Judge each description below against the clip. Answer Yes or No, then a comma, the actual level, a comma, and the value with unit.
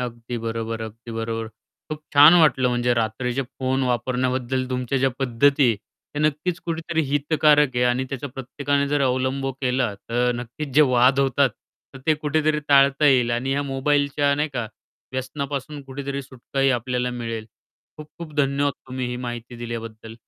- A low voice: Yes, low, 130 Hz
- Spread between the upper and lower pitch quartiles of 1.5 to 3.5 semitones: Yes, average, 2.7 semitones